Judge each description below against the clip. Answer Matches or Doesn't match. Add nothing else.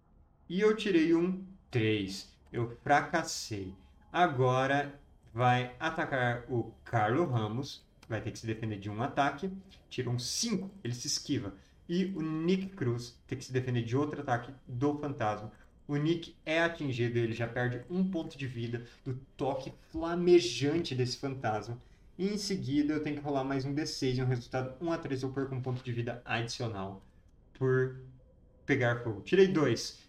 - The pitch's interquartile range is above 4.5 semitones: Matches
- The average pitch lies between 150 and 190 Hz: Doesn't match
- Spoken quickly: Doesn't match